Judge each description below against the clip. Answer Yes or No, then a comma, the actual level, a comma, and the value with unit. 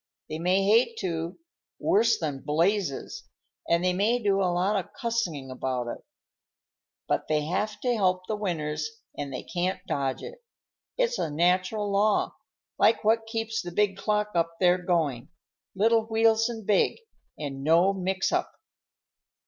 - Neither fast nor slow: Yes, average, 155 wpm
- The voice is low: No, high, 190 Hz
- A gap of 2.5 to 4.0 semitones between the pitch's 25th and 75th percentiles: No, average, 4.7 semitones